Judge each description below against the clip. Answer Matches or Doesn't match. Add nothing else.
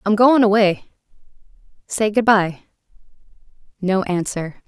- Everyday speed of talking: Doesn't match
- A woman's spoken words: Matches